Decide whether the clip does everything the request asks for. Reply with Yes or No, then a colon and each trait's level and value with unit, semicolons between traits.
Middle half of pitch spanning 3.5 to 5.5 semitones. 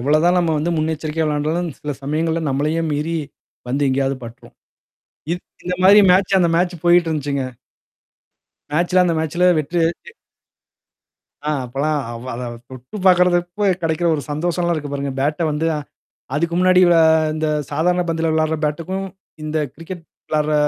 No: average, 3.0 semitones